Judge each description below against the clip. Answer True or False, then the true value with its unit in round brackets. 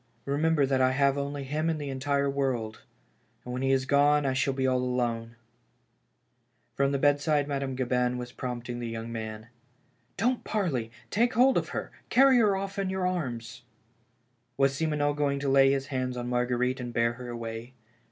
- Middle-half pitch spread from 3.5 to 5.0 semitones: False (2.9 semitones)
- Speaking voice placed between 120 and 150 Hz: True (135 Hz)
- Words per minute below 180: False (190 wpm)